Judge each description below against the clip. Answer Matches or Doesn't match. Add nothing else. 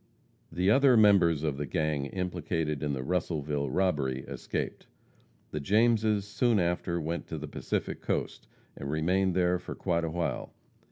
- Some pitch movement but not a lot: Matches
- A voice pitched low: Matches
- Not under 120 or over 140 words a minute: Doesn't match